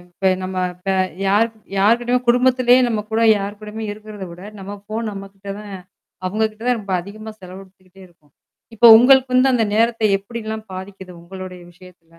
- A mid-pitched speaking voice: No, high, 205 Hz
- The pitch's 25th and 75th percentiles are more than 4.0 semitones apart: No, average, 3.3 semitones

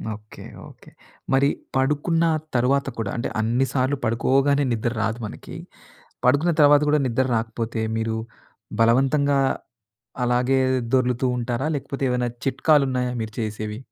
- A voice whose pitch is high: No, low, 125 Hz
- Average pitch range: Yes, average, 3.2 semitones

